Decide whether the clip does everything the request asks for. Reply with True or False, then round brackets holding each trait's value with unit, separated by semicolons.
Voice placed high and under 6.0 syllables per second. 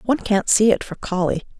True (205 Hz; 5.8 syllables/s)